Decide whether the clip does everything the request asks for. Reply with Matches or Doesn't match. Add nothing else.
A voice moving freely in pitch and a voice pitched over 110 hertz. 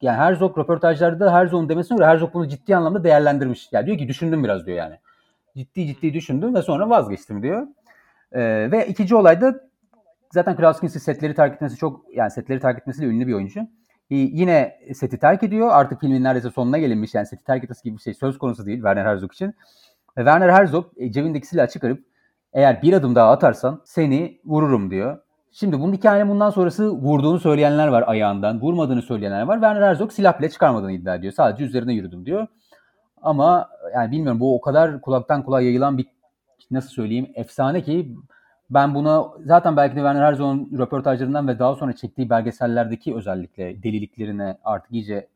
Matches